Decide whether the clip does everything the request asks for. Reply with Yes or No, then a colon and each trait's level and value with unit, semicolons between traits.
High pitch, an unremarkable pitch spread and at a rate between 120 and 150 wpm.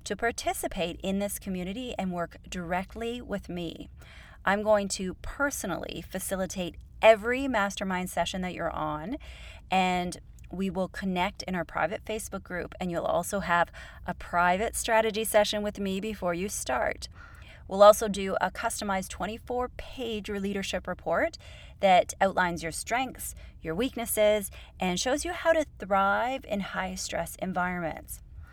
Yes: high, 195 Hz; average, 3.4 semitones; average, 140 wpm